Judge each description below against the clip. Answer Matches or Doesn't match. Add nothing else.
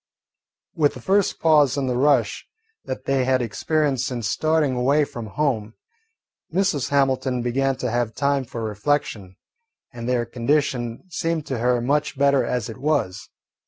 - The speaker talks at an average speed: Matches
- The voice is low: Matches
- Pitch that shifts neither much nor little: Matches